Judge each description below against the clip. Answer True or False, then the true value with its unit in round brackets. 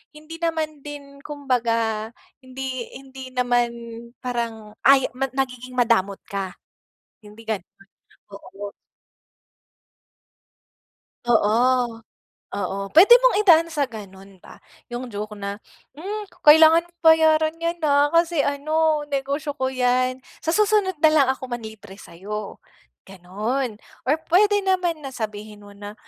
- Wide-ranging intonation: True (6.3 semitones)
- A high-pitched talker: True (260 Hz)